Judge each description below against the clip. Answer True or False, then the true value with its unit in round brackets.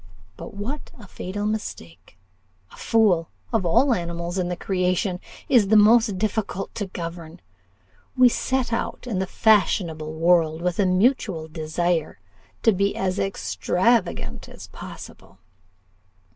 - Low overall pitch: False (185 Hz)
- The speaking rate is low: True (130 wpm)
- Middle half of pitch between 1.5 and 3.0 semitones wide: False (4.2 semitones)